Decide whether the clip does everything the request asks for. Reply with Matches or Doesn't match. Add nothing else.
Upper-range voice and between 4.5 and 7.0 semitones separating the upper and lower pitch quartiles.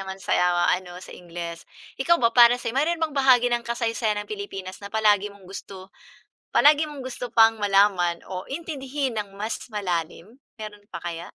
Matches